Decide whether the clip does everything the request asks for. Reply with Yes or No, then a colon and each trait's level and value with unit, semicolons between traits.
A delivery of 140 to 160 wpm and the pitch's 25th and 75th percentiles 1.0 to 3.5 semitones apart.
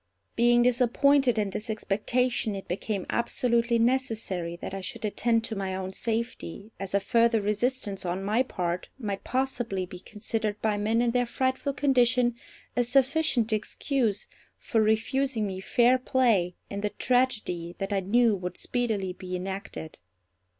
No: average, 150 wpm; average, 4.0 semitones